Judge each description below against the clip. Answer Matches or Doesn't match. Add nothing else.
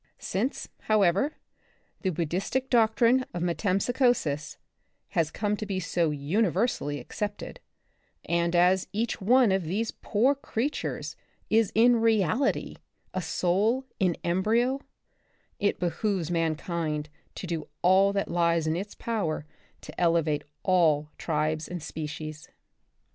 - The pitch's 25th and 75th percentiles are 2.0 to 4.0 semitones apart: Doesn't match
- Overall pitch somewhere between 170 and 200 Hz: Matches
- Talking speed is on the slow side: Matches